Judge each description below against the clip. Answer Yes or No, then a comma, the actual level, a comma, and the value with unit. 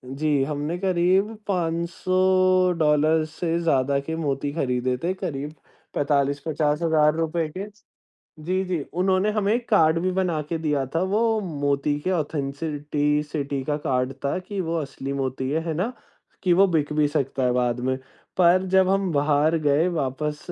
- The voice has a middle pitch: Yes, medium, 155 Hz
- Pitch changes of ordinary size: Yes, average, 4.2 semitones